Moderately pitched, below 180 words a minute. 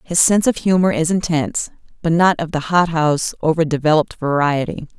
Yes: medium, 160 Hz; average, 155 wpm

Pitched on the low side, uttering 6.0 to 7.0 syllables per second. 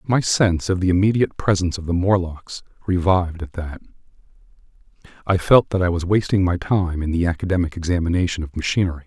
Yes: very low, 90 Hz; 6.3 syllables/s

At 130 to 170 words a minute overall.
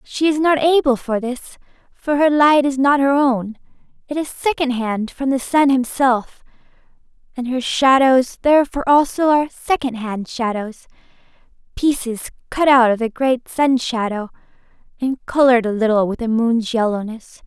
Yes: average, 150 wpm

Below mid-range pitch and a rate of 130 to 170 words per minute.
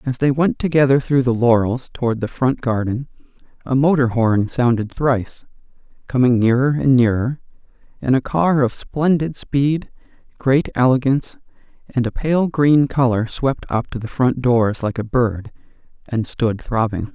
Yes: low, 125 Hz; average, 155 wpm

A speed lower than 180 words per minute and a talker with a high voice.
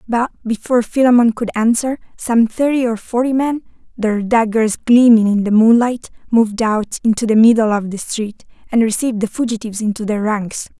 Yes: average, 170 wpm; high, 225 Hz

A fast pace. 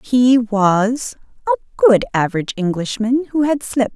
No: slow, 135 wpm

